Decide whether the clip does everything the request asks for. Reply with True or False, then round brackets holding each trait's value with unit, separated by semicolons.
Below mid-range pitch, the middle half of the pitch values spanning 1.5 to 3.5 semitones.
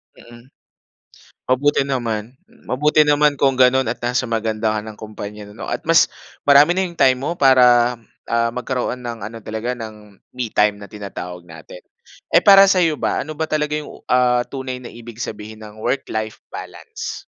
False (120 Hz; 4.1 semitones)